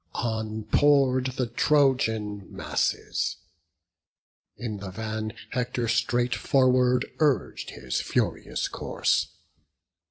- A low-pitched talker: Yes, low, 120 Hz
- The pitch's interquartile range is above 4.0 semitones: No, average, 2.9 semitones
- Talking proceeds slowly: Yes, slow, 90 wpm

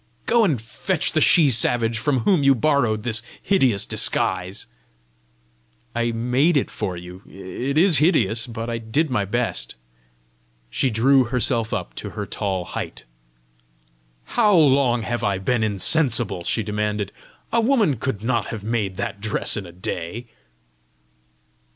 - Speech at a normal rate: Yes, average, 145 wpm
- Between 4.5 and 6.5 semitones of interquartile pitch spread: Yes, average, 4.8 semitones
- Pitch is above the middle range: No, low, 115 Hz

